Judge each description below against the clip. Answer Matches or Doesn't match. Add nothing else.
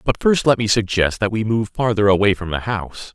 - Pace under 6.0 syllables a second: Matches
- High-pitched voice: Doesn't match